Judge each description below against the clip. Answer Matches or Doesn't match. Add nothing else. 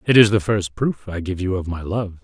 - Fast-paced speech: Matches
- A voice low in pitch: Matches